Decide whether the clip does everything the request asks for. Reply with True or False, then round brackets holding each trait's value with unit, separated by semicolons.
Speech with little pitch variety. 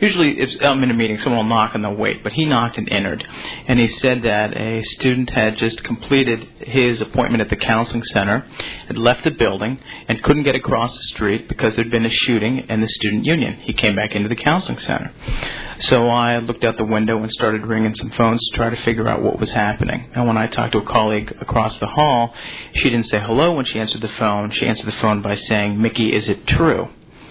True (2.0 semitones)